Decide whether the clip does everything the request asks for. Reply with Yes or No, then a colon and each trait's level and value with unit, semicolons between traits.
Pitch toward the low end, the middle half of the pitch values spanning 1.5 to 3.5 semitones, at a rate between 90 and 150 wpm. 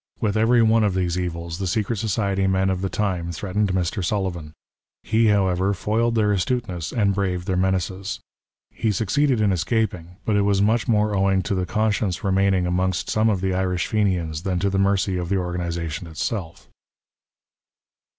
No: very low, 95 Hz; average, 2.7 semitones; average, 180 wpm